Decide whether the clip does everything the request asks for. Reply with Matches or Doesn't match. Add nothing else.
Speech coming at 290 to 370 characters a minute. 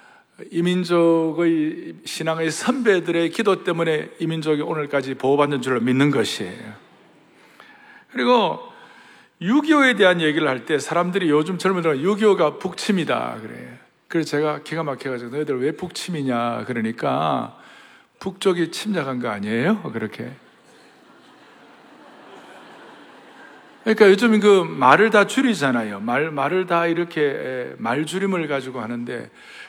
Doesn't match